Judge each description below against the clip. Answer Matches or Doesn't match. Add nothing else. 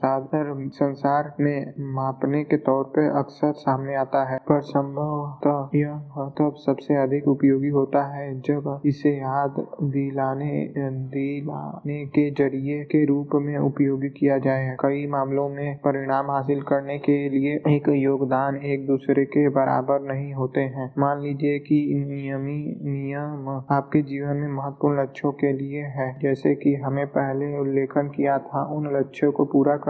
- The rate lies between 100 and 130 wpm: Doesn't match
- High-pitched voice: Doesn't match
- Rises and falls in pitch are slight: Matches